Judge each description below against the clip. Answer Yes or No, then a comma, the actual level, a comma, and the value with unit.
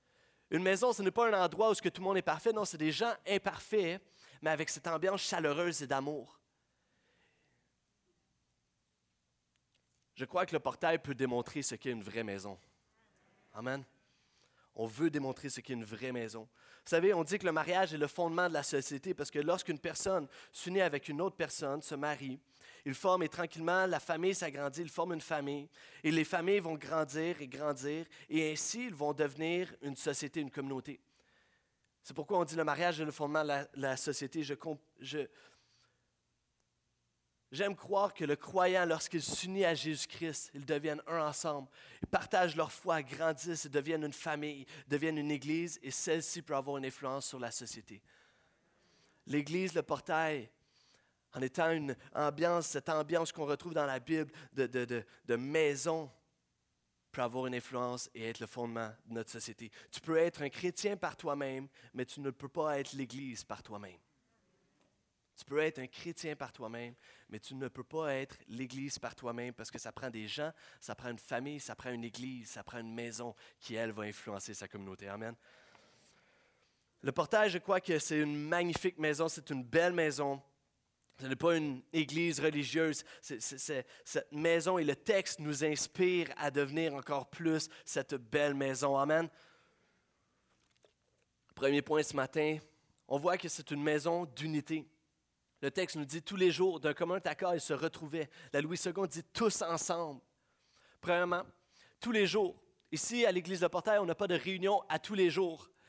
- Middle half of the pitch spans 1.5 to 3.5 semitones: No, average, 4.1 semitones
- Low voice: No, medium, 150 Hz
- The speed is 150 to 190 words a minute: Yes, average, 180 wpm